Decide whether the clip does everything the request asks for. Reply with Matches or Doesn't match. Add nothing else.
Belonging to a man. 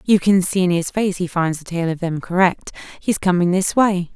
Doesn't match